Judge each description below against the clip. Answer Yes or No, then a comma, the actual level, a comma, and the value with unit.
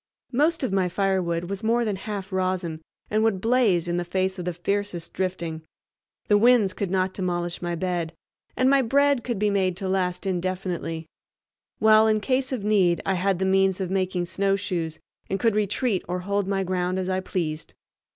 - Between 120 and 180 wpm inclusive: No, average, 190 wpm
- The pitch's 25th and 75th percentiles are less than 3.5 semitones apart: Yes, narrow, 2.6 semitones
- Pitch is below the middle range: No, high, 190 Hz